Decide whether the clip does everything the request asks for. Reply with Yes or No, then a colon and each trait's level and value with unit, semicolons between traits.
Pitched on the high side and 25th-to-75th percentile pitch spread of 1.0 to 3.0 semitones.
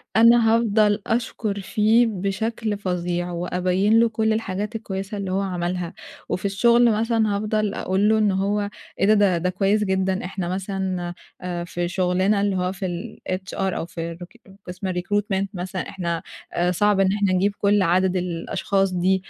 Yes: high, 195 Hz; narrow, 2.5 semitones